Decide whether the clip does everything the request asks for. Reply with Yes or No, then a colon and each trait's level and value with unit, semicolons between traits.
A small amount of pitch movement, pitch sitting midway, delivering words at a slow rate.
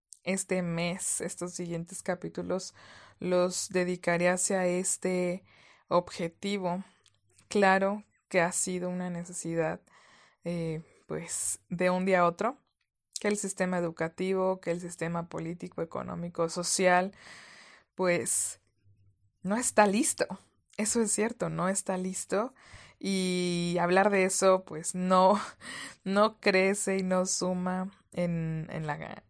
Yes: narrow, 2.0 semitones; medium, 180 Hz; slow, 115 wpm